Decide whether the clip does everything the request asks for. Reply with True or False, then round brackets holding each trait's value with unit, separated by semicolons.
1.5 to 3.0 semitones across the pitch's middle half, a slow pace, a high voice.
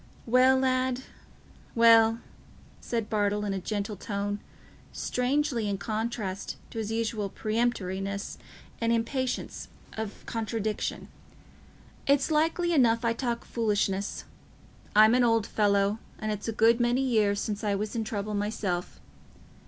True (2.6 semitones; 130 wpm; 225 Hz)